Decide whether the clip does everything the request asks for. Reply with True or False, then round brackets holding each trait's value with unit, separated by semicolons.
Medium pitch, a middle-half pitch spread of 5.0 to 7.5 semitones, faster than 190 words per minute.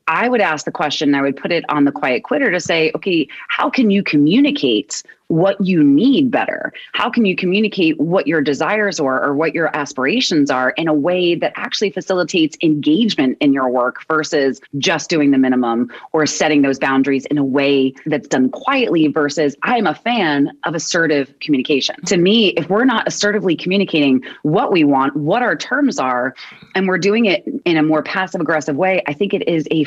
True (160 Hz; 5.5 semitones; 200 wpm)